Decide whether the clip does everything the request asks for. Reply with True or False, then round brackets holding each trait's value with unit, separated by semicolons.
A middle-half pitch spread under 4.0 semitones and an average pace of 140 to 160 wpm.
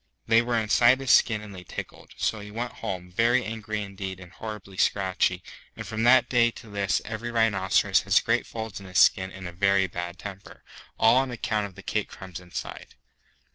False (3.1 semitones; 200 wpm)